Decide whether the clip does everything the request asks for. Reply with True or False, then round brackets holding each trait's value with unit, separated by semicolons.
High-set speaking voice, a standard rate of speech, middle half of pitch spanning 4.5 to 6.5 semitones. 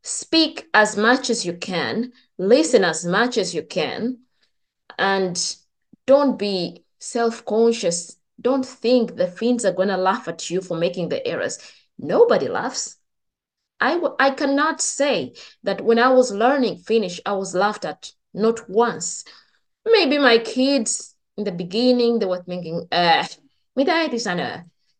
True (230 Hz; 145 wpm; 5.4 semitones)